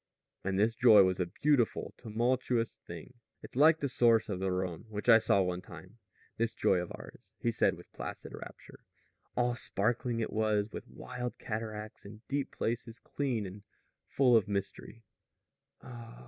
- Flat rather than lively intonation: No, average, 3.5 semitones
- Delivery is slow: No, average, 160 wpm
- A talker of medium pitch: No, low, 110 Hz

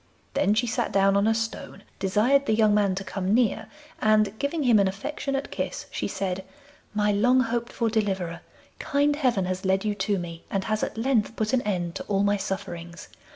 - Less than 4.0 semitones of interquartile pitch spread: Yes, average, 3.3 semitones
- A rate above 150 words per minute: Yes, average, 200 wpm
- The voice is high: Yes, high, 210 Hz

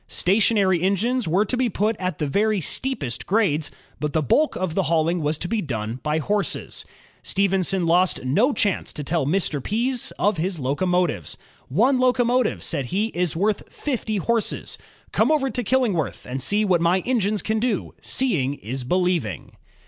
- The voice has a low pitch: No, medium, 185 Hz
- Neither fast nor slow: Yes, average, 175 wpm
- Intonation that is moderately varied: No, wide, 5.8 semitones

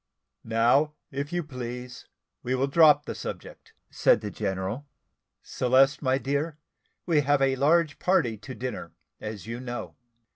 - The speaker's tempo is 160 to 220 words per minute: No, average, 145 wpm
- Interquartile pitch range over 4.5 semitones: No, average, 3.3 semitones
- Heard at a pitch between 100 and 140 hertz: Yes, low, 135 Hz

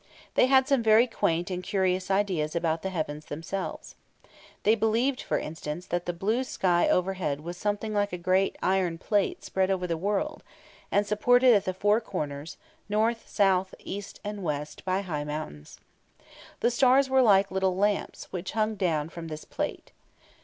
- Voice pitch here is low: No, high, 190 Hz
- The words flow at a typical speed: Yes, average, 170 wpm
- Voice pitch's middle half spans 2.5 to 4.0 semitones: Yes, average, 3.7 semitones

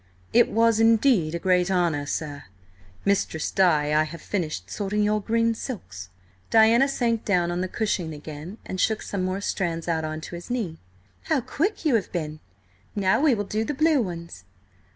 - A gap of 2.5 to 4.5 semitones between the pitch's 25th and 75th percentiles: No, wide, 5.6 semitones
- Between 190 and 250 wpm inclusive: No, average, 180 wpm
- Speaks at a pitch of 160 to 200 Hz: Yes, high, 190 Hz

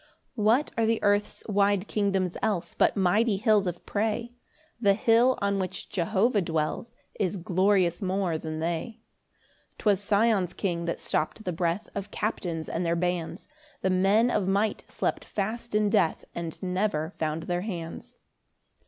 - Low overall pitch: No, high, 195 Hz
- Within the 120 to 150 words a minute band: No, average, 160 wpm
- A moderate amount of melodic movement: Yes, average, 3.6 semitones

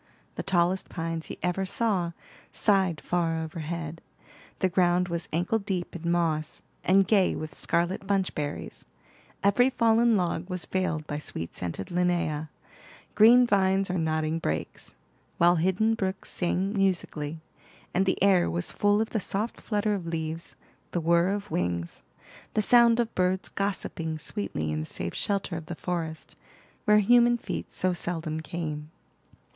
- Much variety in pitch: No, average, 3.5 semitones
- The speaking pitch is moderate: Yes, medium, 180 Hz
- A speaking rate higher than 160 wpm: No, average, 150 wpm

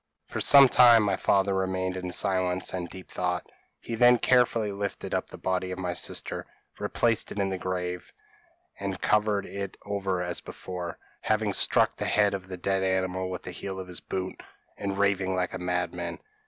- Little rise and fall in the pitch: Yes, narrow, 1.7 semitones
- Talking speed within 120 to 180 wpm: No, average, 190 wpm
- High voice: No, very low, 95 Hz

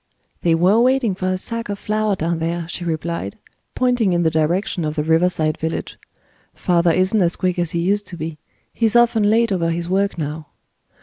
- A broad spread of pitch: No, average, 3.9 semitones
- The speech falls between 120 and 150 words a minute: No, average, 200 wpm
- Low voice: No, medium, 175 Hz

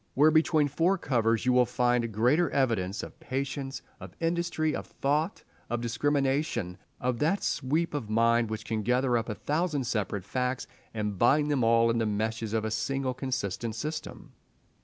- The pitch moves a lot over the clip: No, average, 4.4 semitones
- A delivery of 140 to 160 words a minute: No, average, 170 wpm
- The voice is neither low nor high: No, low, 125 Hz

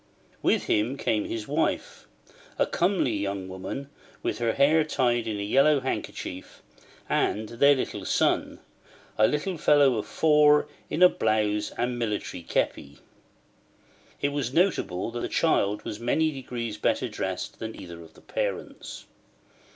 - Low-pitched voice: Yes, low, 120 Hz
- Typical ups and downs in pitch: No, wide, 5.8 semitones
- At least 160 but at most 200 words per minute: No, average, 145 wpm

